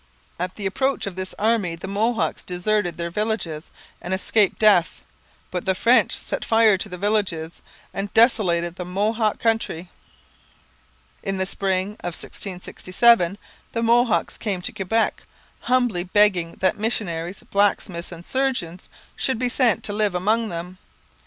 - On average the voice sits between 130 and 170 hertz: No, high, 195 Hz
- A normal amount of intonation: Yes, average, 3.8 semitones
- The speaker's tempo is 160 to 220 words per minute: No, average, 145 wpm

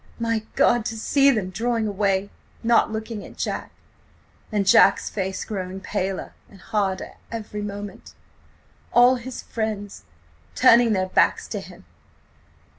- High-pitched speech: Yes, high, 210 Hz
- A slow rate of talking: Yes, slow, 120 wpm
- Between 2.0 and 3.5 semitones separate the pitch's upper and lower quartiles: Yes, average, 2.8 semitones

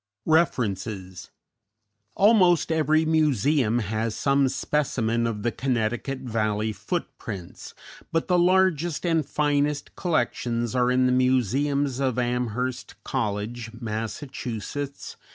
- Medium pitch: No, low, 125 Hz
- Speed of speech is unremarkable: No, slow, 100 wpm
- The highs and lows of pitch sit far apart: No, average, 4.7 semitones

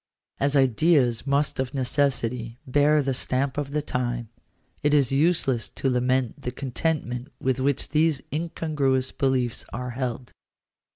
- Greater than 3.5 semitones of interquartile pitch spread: No, narrow, 2.5 semitones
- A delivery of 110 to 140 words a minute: Yes, slow, 135 wpm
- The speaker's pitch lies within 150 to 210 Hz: No, low, 130 Hz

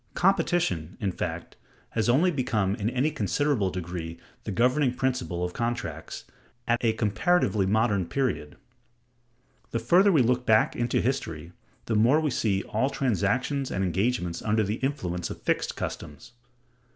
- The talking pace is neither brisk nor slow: Yes, average, 145 wpm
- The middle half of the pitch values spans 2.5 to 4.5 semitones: No, wide, 5.6 semitones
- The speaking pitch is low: Yes, low, 115 Hz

